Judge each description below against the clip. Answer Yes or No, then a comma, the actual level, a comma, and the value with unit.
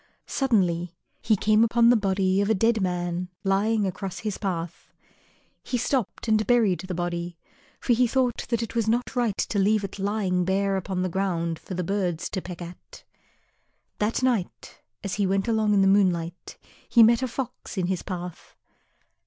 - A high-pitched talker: Yes, high, 195 Hz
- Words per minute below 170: No, average, 180 wpm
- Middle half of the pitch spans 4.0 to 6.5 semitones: No, average, 3.6 semitones